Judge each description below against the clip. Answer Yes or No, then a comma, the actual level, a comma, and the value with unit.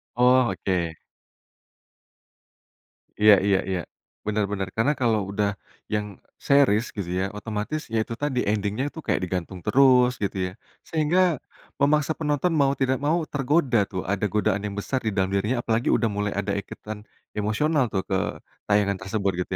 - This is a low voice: Yes, low, 110 Hz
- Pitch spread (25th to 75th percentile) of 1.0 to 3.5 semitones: No, average, 5.0 semitones